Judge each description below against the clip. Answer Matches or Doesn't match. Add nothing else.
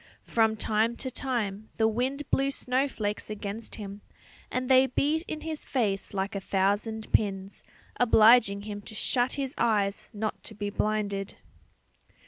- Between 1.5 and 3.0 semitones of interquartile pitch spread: Doesn't match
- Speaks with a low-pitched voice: Doesn't match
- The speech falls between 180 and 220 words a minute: Doesn't match